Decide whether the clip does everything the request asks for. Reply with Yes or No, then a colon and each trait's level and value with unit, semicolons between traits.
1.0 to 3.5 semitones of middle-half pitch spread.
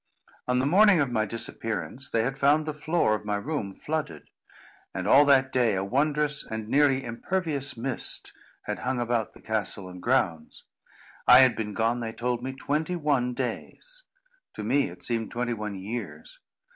No: average, 4.5 semitones